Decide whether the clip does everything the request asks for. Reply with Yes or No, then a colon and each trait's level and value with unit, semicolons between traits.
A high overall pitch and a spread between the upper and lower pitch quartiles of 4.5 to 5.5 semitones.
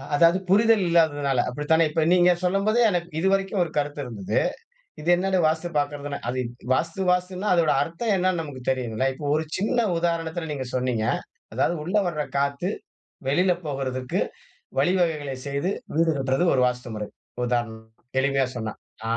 No: medium, 160 Hz; average, 5.0 semitones